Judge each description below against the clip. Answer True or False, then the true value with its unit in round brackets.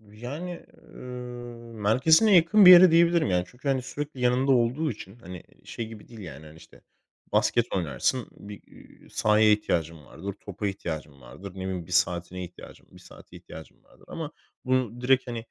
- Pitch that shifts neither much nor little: False (5.7 semitones)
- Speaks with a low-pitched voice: True (115 Hz)